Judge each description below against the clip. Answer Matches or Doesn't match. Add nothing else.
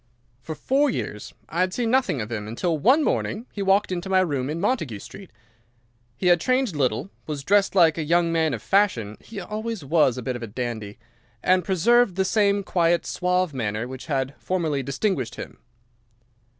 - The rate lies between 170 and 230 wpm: Matches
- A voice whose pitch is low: Doesn't match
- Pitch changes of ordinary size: Doesn't match